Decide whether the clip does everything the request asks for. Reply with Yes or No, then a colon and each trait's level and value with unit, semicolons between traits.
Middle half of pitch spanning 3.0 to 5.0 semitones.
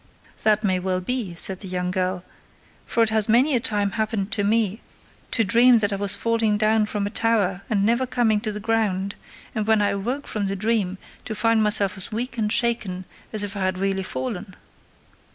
No: narrow, 2.6 semitones